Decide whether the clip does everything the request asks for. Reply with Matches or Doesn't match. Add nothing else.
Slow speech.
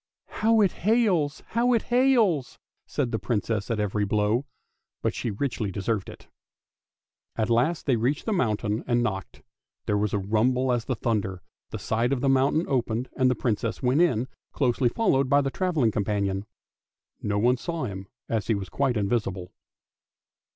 Doesn't match